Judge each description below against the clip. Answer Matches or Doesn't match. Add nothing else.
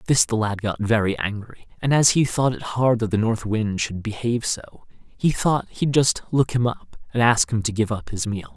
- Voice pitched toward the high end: Doesn't match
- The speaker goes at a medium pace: Doesn't match